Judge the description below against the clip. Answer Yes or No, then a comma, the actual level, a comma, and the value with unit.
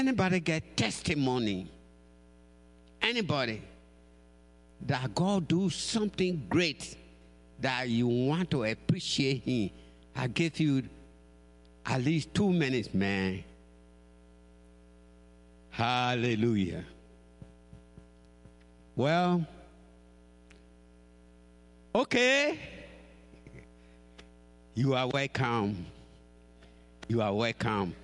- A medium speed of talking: No, slow, 70 wpm